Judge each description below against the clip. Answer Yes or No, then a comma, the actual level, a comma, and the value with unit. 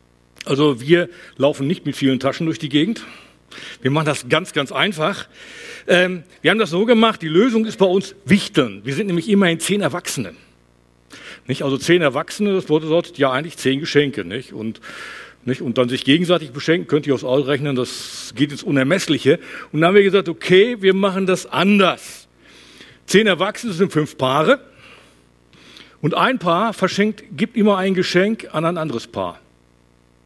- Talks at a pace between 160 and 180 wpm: Yes, average, 175 wpm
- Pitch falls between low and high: Yes, medium, 160 Hz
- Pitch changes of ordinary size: No, wide, 6.3 semitones